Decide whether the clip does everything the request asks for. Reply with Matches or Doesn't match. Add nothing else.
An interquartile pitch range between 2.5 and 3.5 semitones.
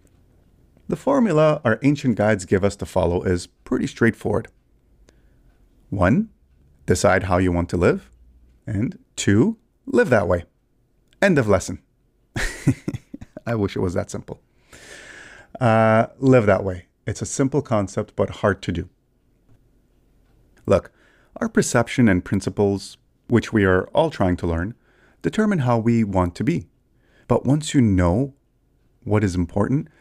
Doesn't match